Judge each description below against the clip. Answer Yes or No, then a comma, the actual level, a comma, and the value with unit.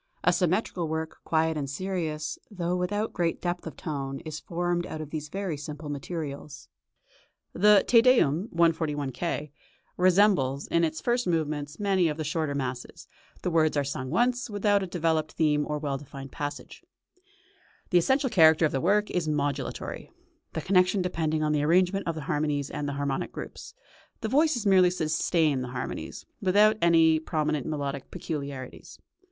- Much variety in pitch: No, average, 3.7 semitones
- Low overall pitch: No, medium, 160 Hz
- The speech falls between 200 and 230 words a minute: No, average, 165 wpm